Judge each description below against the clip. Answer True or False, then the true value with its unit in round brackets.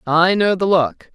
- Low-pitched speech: False (185 Hz)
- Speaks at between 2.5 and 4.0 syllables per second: True (3.9 syllables/s)